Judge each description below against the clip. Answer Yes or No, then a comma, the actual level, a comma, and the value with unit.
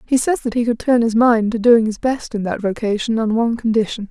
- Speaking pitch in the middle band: No, high, 230 Hz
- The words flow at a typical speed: No, fast, 265 wpm